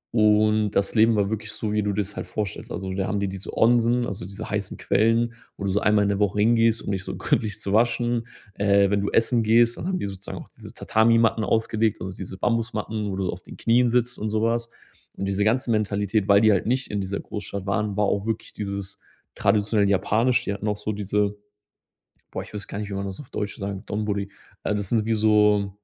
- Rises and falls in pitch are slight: Yes, narrow, 2.1 semitones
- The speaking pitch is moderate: No, low, 105 Hz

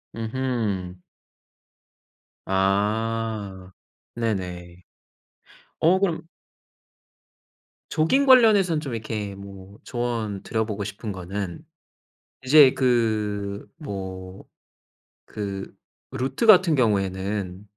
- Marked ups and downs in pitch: No, average, 4.8 semitones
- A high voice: No, low, 105 Hz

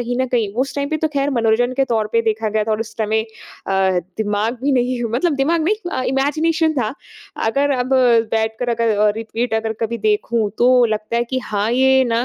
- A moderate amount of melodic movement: Yes, average, 3.6 semitones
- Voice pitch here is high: Yes, high, 235 Hz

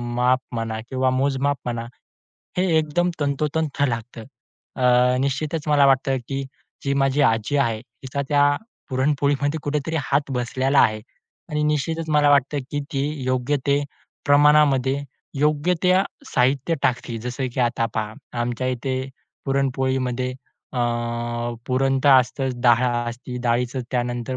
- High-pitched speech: No, low, 135 Hz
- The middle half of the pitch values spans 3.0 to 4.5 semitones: No, narrow, 2.6 semitones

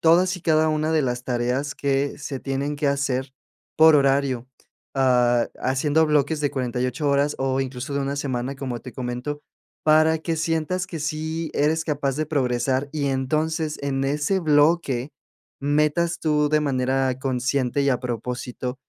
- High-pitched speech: No, medium, 140 Hz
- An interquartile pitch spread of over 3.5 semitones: No, average, 2.9 semitones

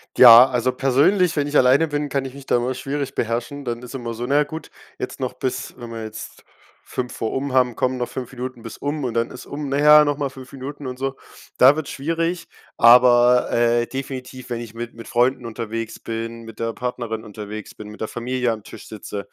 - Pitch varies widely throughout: No, average, 2.8 semitones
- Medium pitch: No, low, 125 Hz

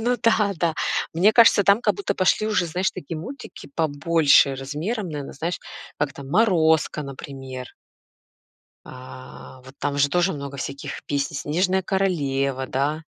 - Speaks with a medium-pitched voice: Yes, medium, 155 Hz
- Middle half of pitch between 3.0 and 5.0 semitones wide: No, wide, 5.4 semitones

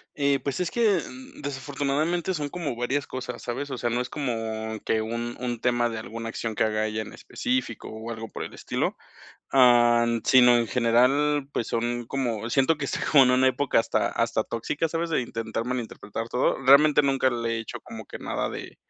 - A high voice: No, low, 125 Hz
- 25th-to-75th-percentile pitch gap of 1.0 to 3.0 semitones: No, average, 3.5 semitones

